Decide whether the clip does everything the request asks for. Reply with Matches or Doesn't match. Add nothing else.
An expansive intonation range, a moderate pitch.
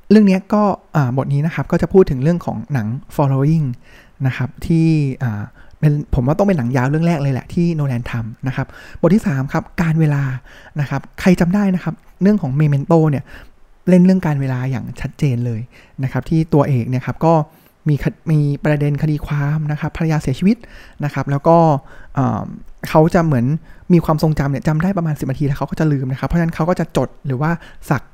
Doesn't match